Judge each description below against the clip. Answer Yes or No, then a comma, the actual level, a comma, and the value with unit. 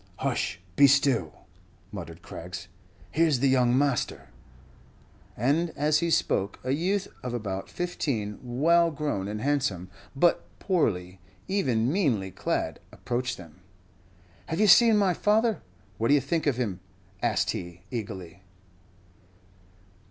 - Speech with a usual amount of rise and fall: No, wide, 8.4 semitones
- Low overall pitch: Yes, low, 130 Hz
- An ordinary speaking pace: No, slow, 130 wpm